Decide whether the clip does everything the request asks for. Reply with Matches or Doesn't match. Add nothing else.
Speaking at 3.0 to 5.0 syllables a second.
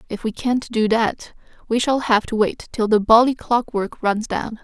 Matches